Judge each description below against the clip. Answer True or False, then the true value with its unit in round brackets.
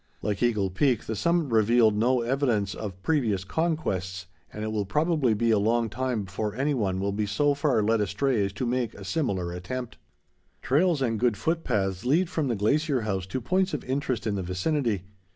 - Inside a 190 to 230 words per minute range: True (200 wpm)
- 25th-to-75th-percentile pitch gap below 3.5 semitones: False (5.4 semitones)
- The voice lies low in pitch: True (115 Hz)